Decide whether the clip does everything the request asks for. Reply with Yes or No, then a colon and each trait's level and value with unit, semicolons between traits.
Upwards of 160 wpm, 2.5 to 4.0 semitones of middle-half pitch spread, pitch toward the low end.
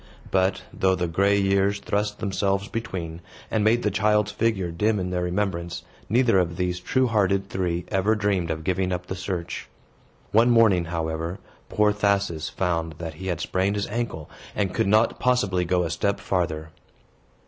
Yes: average, 170 wpm; average, 2.9 semitones; very low, 95 Hz